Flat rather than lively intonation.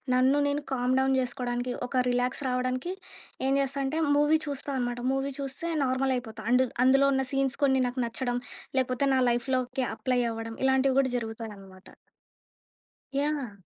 Yes: narrow, 1.7 semitones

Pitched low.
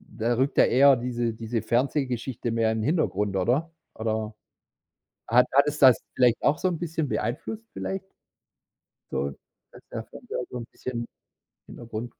Yes: low, 120 Hz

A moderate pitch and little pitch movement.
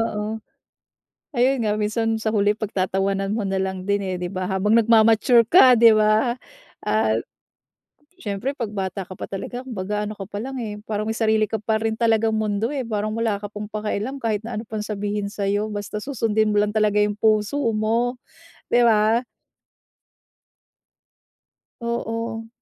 No: high, 215 Hz; narrow, 1.8 semitones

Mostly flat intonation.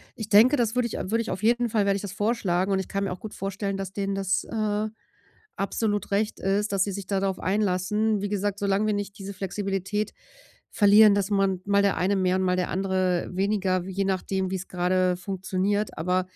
Yes: narrow, 1.8 semitones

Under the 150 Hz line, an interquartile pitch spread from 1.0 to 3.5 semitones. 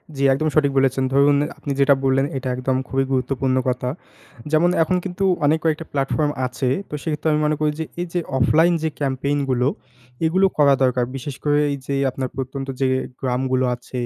Yes: medium, 140 Hz; average, 2.7 semitones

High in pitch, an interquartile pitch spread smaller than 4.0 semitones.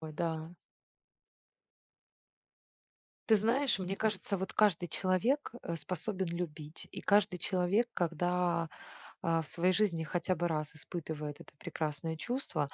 No: medium, 175 Hz; average, 3.3 semitones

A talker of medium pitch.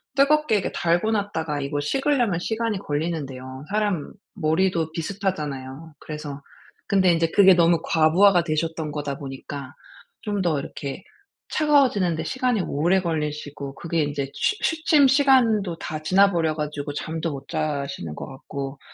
Yes: medium, 165 Hz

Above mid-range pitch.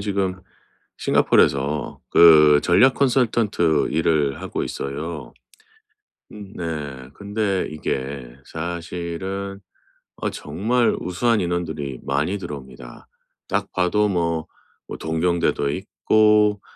No: very low, 85 Hz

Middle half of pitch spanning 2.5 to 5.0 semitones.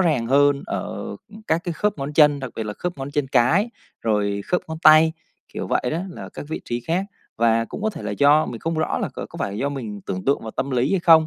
No: wide, 5.4 semitones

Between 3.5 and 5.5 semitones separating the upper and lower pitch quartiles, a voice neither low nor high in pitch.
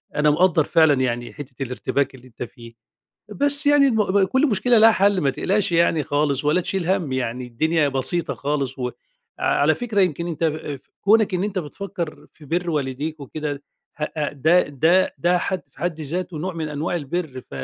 Yes: average, 4.7 semitones; medium, 160 Hz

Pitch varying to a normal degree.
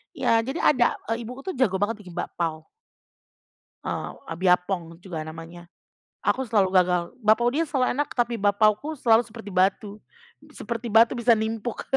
Yes: average, 4.5 semitones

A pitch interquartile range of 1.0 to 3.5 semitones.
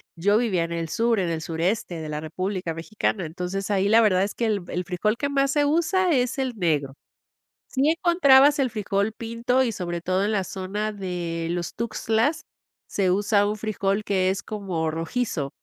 No: average, 4.7 semitones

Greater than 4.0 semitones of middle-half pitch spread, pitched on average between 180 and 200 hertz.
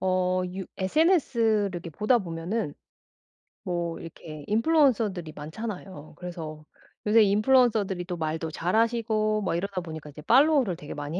Yes: average, 5.1 semitones; medium, 185 Hz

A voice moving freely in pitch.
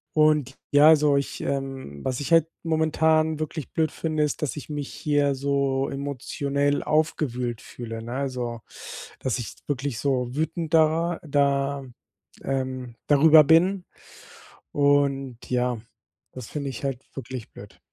No: average, 2.9 semitones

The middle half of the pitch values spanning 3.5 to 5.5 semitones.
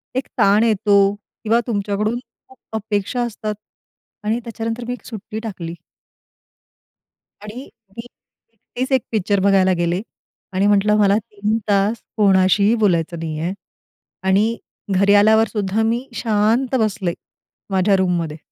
No: narrow, 2.6 semitones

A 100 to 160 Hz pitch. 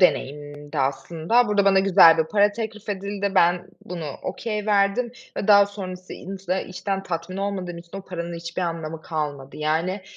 No: medium, 185 Hz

